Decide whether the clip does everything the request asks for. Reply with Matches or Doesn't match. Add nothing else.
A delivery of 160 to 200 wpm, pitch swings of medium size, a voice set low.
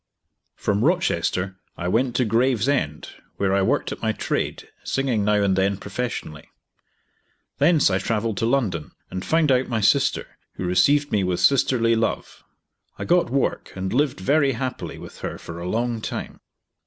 Doesn't match